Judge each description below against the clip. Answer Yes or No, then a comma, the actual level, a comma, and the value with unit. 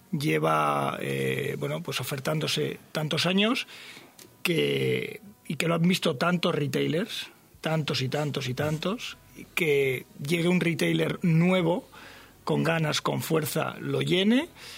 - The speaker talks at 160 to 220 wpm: No, average, 130 wpm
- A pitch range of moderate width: Yes, average, 3.5 semitones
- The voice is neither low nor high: Yes, medium, 160 Hz